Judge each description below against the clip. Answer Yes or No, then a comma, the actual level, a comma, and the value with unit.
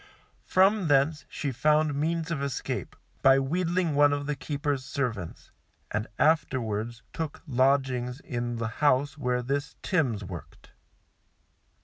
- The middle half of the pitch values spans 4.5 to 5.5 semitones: No, average, 3.6 semitones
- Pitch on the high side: No, medium, 140 Hz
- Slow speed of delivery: Yes, slow, 125 wpm